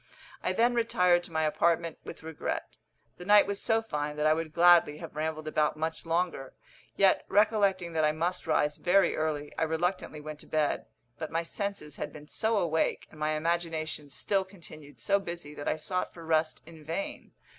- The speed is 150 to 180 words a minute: No, average, 190 wpm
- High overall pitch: No, medium, 165 Hz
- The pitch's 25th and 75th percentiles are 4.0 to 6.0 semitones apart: No, average, 2.9 semitones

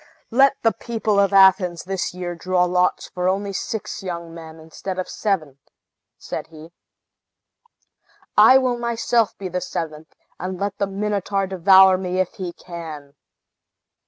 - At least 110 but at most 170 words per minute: Yes, average, 145 wpm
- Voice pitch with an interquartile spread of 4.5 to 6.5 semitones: No, average, 2.7 semitones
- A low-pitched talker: No, medium, 185 Hz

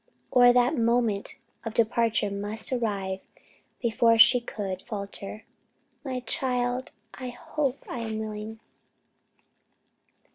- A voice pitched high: Yes, high, 230 Hz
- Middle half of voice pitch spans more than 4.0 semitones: No, average, 2.7 semitones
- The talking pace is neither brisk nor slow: No, slow, 110 wpm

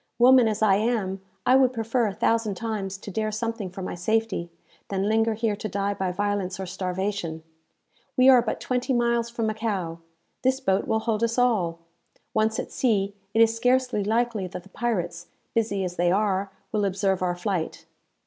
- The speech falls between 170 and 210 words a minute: Yes, average, 185 wpm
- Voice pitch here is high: Yes, high, 215 Hz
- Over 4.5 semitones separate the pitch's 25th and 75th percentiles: No, average, 3.1 semitones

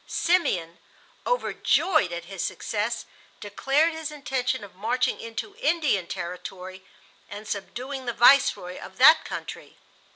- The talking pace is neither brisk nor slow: No, slow, 120 wpm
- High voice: Yes, high, 230 Hz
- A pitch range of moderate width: No, wide, 6.9 semitones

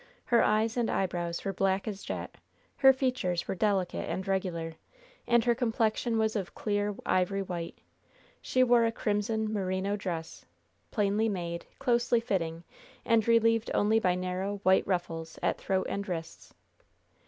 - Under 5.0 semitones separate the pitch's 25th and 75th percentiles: Yes, average, 3.6 semitones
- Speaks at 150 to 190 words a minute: Yes, average, 155 wpm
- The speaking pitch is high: Yes, high, 200 Hz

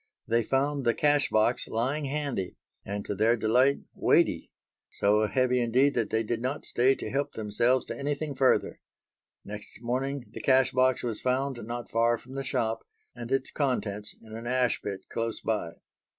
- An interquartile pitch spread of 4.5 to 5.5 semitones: No, average, 3.2 semitones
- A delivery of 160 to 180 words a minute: Yes, average, 175 wpm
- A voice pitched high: No, low, 120 Hz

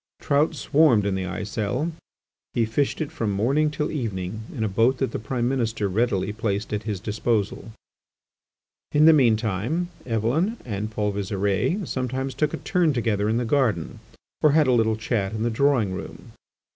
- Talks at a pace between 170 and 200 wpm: Yes, average, 175 wpm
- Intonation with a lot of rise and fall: No, average, 5.0 semitones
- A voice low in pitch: Yes, low, 115 Hz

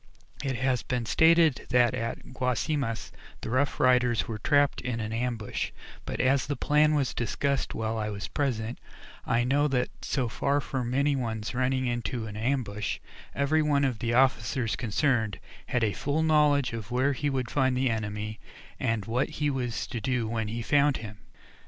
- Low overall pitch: Yes, low, 125 Hz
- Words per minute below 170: No, average, 175 wpm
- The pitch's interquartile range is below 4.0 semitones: Yes, average, 3.6 semitones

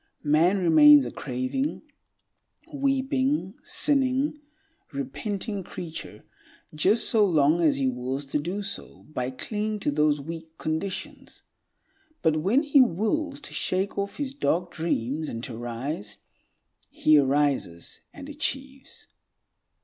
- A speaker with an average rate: No, slow, 120 wpm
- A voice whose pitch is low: No, medium, 170 Hz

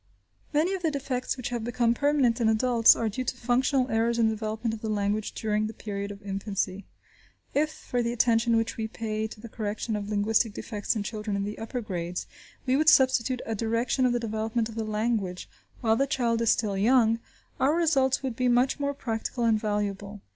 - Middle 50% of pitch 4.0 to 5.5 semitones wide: No, average, 2.8 semitones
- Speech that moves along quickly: Yes, fast, 210 wpm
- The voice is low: No, high, 225 Hz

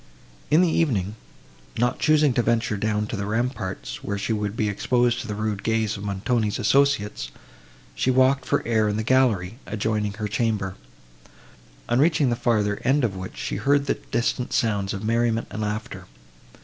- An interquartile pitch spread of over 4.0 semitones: No, average, 3.0 semitones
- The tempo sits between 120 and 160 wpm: No, average, 175 wpm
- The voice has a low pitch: Yes, low, 110 Hz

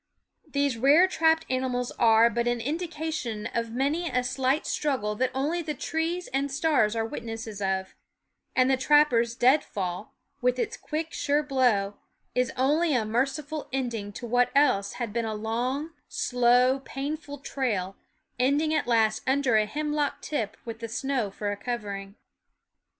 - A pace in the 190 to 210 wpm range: No, average, 155 wpm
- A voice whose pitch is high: Yes, very high, 255 Hz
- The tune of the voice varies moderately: Yes, average, 4.4 semitones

